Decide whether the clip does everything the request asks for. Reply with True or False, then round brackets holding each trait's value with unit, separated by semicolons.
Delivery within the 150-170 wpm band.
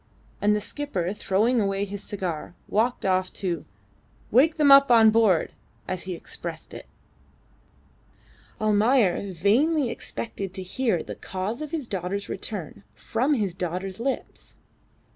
False (140 wpm)